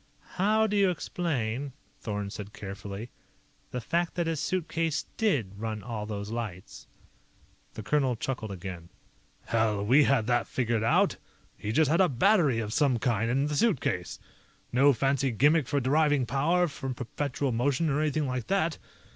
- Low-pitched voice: Yes, low, 130 Hz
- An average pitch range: No, wide, 5.7 semitones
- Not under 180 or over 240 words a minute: No, average, 160 wpm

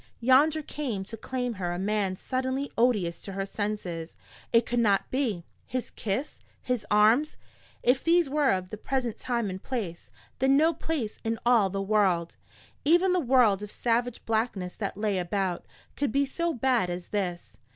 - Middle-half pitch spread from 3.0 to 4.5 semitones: No, average, 5.1 semitones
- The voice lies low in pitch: No, high, 225 Hz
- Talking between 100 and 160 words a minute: No, average, 170 wpm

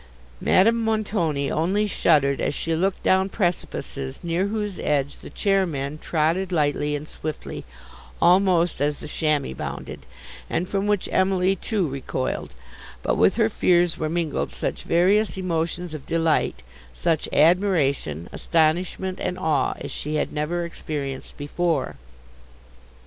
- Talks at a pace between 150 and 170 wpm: No, slow, 135 wpm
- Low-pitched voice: No, medium, 170 Hz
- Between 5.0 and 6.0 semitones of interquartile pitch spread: No, average, 3.9 semitones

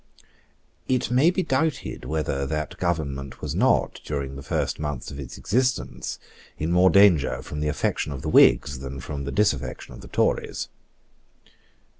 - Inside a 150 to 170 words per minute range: Yes, average, 160 wpm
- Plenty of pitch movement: Yes, wide, 5.8 semitones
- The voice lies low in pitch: Yes, very low, 75 Hz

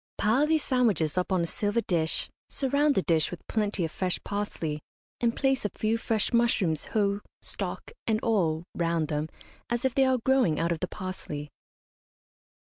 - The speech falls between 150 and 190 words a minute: Yes, average, 175 wpm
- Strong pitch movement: Yes, wide, 6.1 semitones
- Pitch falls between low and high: No, high, 205 Hz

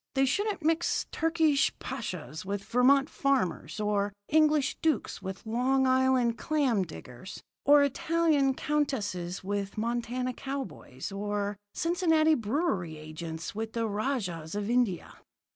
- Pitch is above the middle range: Yes, high, 240 Hz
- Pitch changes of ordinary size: No, wide, 6.0 semitones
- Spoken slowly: Yes, slow, 120 wpm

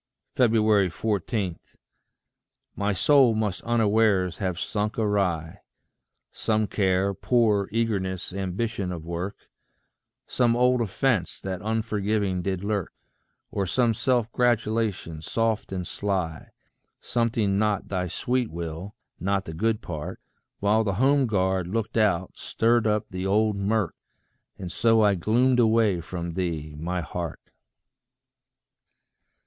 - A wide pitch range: No, average, 3.5 semitones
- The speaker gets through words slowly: Yes, slow, 120 wpm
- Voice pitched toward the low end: Yes, low, 100 Hz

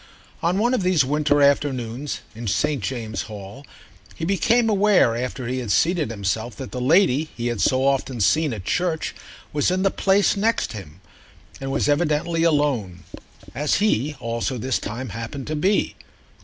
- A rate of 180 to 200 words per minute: No, average, 170 wpm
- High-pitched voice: No, medium, 140 Hz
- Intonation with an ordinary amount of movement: No, wide, 6.1 semitones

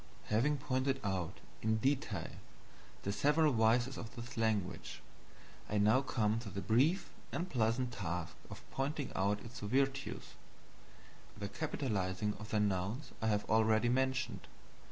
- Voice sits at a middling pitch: No, low, 115 Hz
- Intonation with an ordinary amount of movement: Yes, average, 4.2 semitones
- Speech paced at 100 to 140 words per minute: Yes, slow, 135 wpm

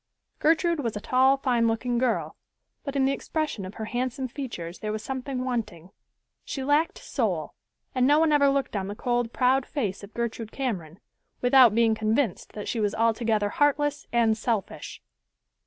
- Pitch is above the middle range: Yes, high, 240 Hz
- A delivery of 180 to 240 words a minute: No, average, 170 wpm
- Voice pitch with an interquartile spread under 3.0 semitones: No, average, 3.9 semitones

